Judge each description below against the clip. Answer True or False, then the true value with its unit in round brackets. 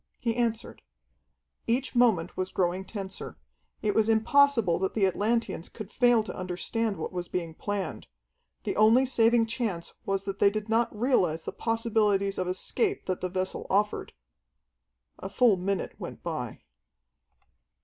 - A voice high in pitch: True (210 Hz)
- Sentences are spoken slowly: False (150 wpm)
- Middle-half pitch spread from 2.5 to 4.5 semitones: True (3.6 semitones)